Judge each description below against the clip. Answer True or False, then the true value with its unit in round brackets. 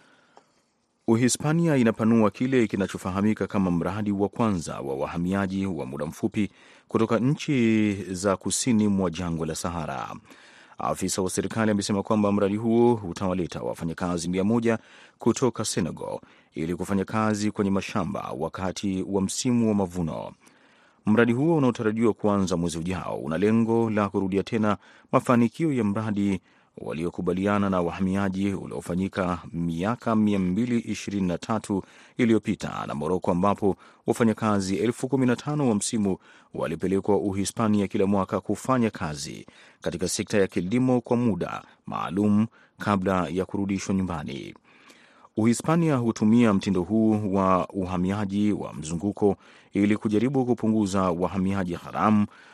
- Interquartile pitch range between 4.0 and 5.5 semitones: False (3.1 semitones)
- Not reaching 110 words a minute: False (115 wpm)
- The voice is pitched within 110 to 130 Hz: False (100 Hz)